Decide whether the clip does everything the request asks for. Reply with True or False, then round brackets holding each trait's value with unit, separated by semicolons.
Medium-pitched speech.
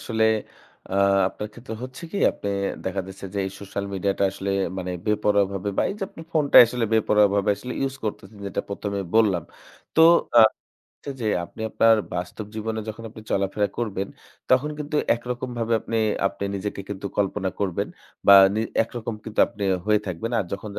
False (105 Hz)